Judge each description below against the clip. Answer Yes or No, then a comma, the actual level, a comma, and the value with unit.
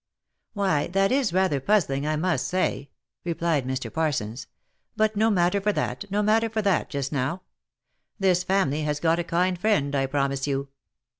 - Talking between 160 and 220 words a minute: Yes, average, 175 wpm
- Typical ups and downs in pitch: No, wide, 5.7 semitones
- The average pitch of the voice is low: No, medium, 170 Hz